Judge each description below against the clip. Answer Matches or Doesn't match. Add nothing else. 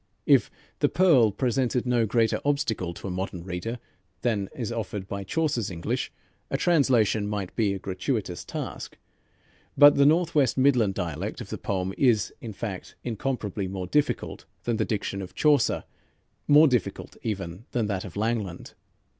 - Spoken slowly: Doesn't match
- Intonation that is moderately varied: Matches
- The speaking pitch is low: Matches